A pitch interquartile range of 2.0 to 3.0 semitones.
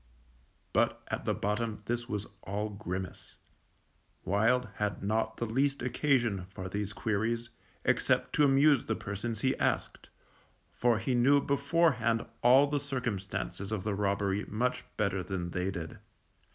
No: average, 4.0 semitones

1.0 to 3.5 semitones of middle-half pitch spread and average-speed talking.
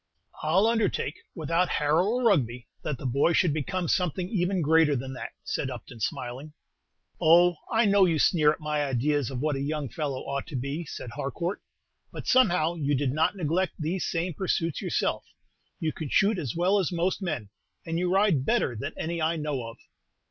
No: average, 4.3 semitones; average, 190 wpm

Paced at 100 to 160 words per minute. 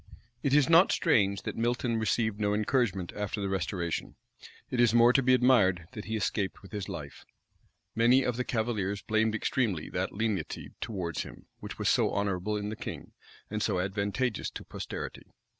No: average, 175 wpm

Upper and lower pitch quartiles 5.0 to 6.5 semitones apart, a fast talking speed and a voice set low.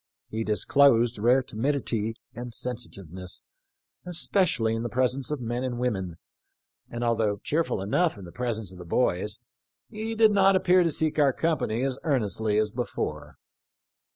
No: average, 5.3 semitones; average, 155 wpm; low, 120 Hz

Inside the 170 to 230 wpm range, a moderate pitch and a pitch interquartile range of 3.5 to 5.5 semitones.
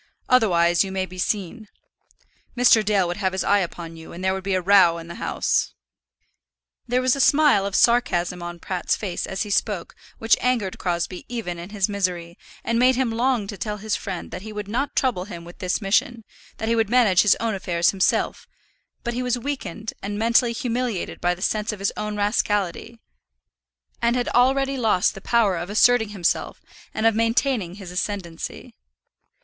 No: average, 190 wpm; high, 205 Hz; average, 4.2 semitones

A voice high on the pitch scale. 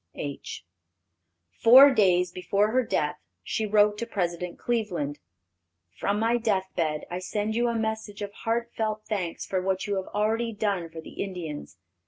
Yes: high, 205 Hz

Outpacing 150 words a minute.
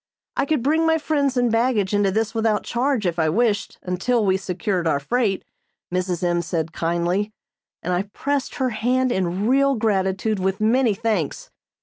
Yes: average, 175 wpm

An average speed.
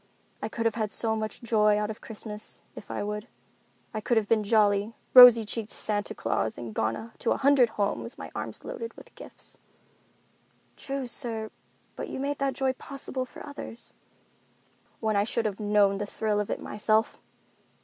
Yes: average, 180 wpm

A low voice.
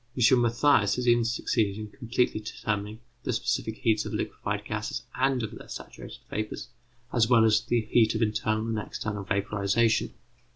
Yes: low, 110 Hz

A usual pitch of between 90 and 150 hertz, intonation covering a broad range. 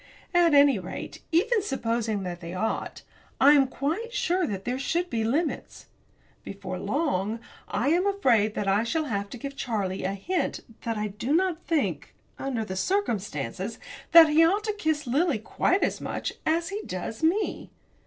No: very high, 270 Hz; wide, 8.0 semitones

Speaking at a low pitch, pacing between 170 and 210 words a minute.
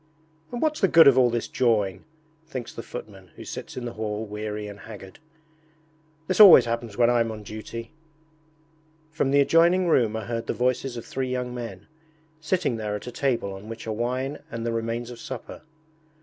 Yes: low, 120 Hz; average, 190 wpm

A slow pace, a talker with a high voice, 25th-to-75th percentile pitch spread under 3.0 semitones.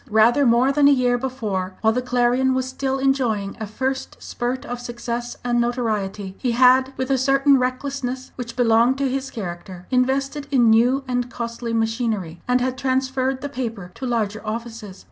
No: average, 175 wpm; high, 245 Hz; narrow, 2.5 semitones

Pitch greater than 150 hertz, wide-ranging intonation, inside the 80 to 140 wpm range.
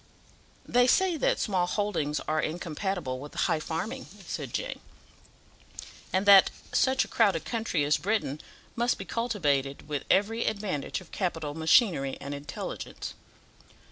Yes: medium, 185 Hz; wide, 6.8 semitones; slow, 135 wpm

